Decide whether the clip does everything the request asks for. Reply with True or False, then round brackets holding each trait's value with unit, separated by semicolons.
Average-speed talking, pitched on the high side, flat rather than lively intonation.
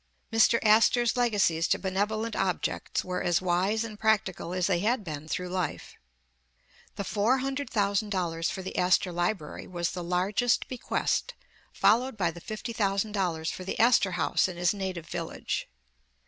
False (160 wpm; 195 Hz; 3.7 semitones)